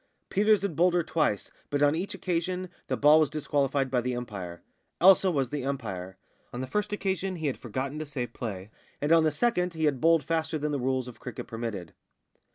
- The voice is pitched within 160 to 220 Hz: No, medium, 145 Hz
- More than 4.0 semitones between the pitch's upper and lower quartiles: Yes, average, 5.1 semitones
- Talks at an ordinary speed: No, fast, 210 wpm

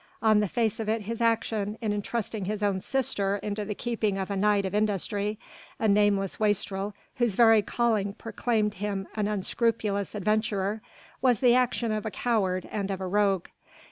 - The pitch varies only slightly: Yes, narrow, 1.9 semitones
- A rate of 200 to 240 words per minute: No, average, 175 wpm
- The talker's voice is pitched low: No, high, 210 Hz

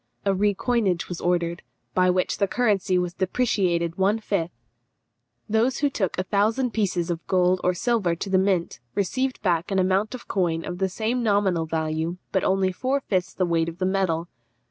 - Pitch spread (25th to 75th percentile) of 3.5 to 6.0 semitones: No, average, 3.0 semitones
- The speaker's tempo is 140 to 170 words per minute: No, average, 185 wpm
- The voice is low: No, medium, 185 Hz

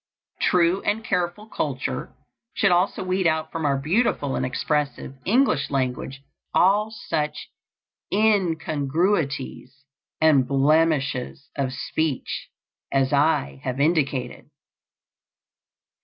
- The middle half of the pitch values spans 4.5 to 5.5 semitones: Yes, average, 4.8 semitones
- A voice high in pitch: No, medium, 155 Hz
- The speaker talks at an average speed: No, slow, 95 wpm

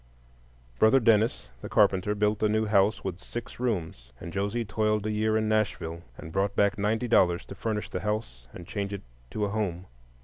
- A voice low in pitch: Yes, low, 105 Hz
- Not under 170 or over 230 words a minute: Yes, average, 190 wpm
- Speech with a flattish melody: Yes, narrow, 2.3 semitones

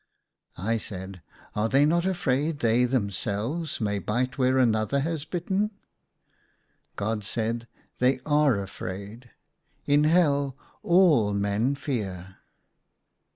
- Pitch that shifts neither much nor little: No, wide, 5.9 semitones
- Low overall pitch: Yes, low, 125 Hz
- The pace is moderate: No, slow, 120 wpm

